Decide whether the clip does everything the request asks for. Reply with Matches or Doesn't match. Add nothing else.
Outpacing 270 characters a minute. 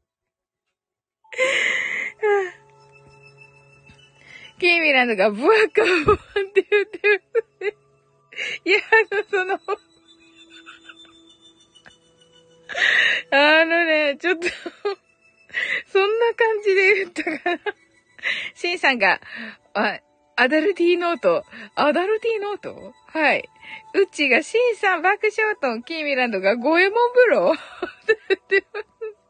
Doesn't match